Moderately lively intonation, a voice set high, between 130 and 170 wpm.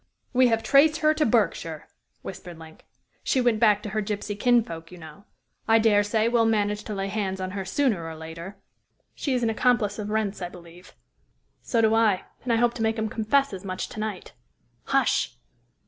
No: average, 3.3 semitones; high, 215 Hz; average, 200 wpm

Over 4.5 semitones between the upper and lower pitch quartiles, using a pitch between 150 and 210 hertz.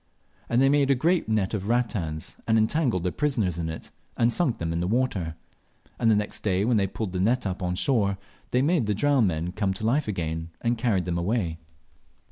No: wide, 5.4 semitones; low, 105 Hz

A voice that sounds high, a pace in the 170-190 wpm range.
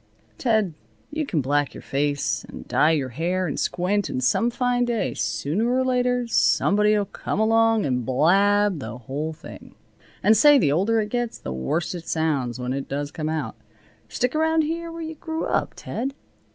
Yes: high, 195 Hz; average, 180 wpm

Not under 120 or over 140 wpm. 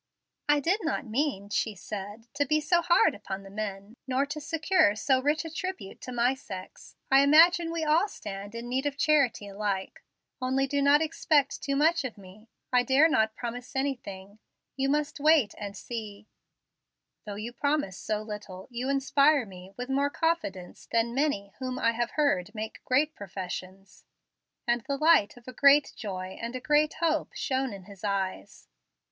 No: average, 175 wpm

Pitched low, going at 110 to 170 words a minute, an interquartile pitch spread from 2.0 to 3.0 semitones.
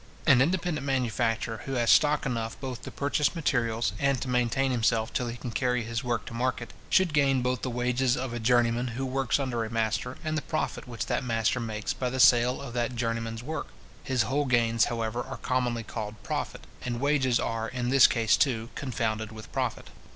No: low, 125 Hz; average, 200 wpm; narrow, 2.5 semitones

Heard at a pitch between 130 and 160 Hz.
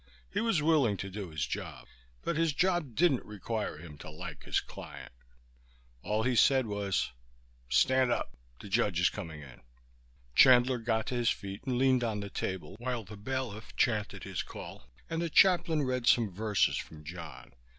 No: low, 110 Hz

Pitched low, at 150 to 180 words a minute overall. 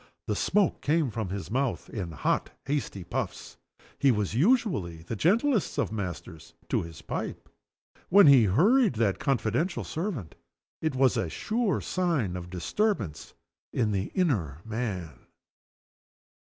No: low, 120 Hz; average, 140 wpm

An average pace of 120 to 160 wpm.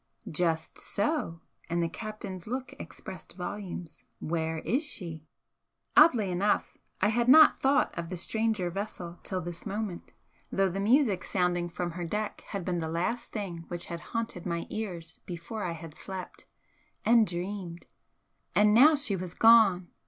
Yes: average, 155 wpm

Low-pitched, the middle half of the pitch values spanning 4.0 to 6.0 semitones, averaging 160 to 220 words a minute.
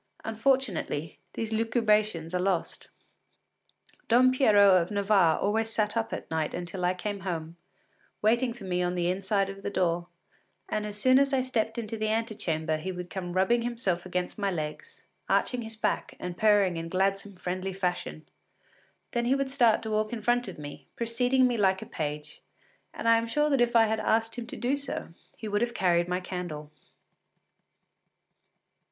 No: high, 205 Hz; average, 4.3 semitones; average, 180 wpm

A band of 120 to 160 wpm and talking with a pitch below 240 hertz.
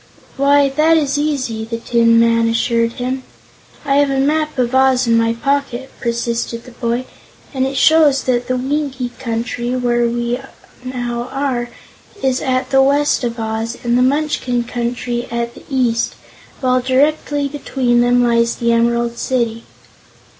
No: average, 155 wpm; high, 245 Hz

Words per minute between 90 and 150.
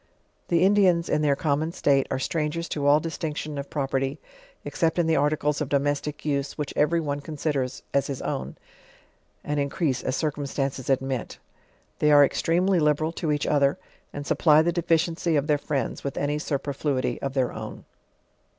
No: average, 170 wpm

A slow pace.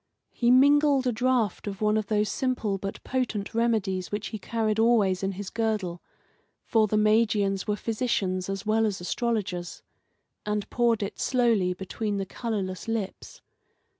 No: average, 155 wpm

